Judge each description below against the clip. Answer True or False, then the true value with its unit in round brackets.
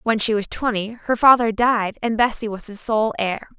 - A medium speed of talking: False (220 wpm)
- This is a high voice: True (220 Hz)